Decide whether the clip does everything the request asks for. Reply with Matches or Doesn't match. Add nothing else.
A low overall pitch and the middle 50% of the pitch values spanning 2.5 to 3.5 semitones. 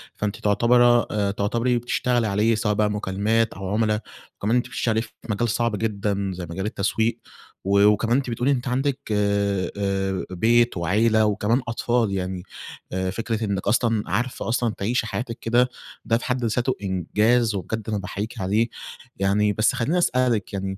Matches